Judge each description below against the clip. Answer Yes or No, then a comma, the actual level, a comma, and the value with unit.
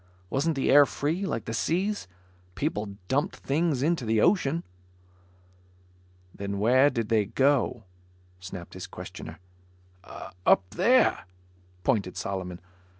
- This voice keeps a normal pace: No, slow, 115 wpm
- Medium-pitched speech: No, low, 130 Hz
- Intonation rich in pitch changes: Yes, wide, 7.7 semitones